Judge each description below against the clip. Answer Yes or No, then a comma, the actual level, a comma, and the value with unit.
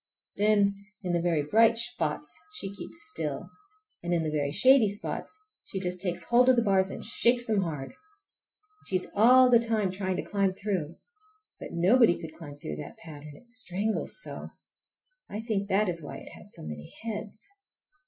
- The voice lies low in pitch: No, high, 200 Hz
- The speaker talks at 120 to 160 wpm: No, average, 185 wpm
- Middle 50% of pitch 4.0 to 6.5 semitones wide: Yes, average, 5.2 semitones